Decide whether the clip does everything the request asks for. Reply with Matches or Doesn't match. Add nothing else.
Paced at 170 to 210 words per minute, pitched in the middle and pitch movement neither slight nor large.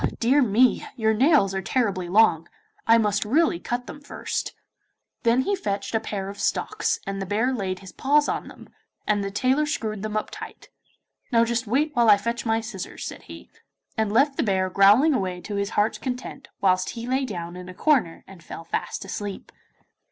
Doesn't match